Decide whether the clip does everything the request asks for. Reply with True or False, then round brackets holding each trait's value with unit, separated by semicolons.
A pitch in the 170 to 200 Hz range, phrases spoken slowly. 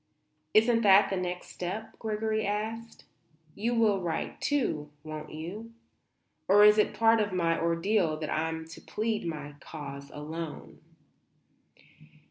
True (190 Hz; 130 wpm)